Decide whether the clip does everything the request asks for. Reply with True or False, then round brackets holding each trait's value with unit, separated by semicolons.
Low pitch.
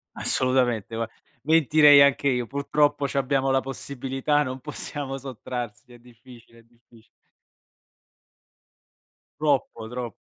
True (130 Hz)